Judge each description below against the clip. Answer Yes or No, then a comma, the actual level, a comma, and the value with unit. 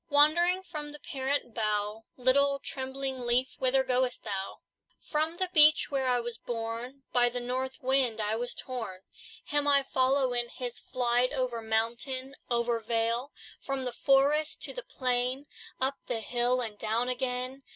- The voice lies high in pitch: Yes, very high, 255 Hz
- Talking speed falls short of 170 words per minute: Yes, average, 160 wpm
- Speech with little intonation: Yes, narrow, 2.3 semitones